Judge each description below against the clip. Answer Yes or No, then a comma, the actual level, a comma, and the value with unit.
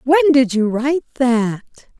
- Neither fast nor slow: Yes, average, 150 wpm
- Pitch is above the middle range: Yes, very high, 255 Hz